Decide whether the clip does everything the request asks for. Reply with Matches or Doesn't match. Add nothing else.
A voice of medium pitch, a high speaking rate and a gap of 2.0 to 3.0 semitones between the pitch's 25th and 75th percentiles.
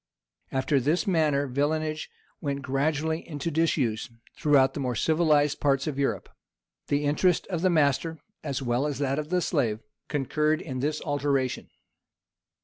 Doesn't match